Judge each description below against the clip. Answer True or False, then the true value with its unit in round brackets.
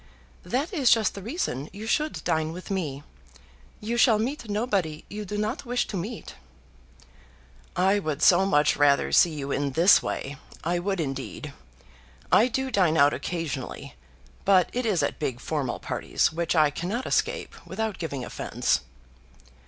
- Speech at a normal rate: True (160 wpm)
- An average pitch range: False (6.4 semitones)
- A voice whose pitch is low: False (180 Hz)